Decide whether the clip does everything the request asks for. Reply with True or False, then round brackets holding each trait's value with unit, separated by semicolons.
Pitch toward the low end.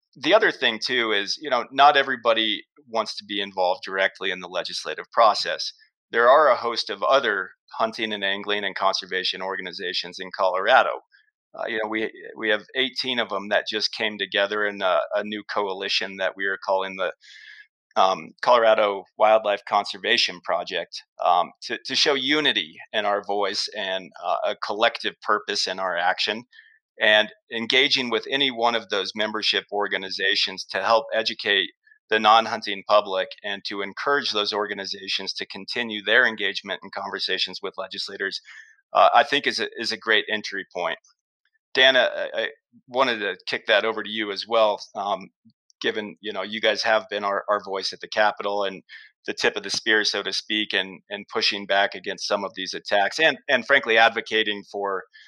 True (105 Hz)